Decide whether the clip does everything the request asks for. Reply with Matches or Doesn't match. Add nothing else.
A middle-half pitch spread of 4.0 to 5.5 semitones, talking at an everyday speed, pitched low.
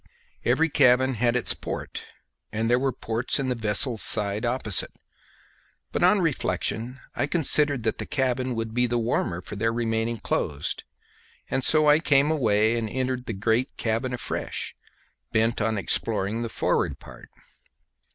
Doesn't match